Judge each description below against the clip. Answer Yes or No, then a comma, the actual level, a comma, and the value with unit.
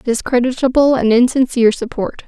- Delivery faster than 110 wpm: No, slow, 105 wpm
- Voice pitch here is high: Yes, high, 245 Hz